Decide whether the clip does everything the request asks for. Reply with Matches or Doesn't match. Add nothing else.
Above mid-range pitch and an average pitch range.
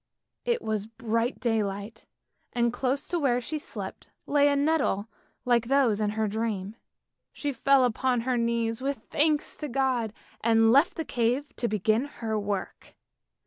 Matches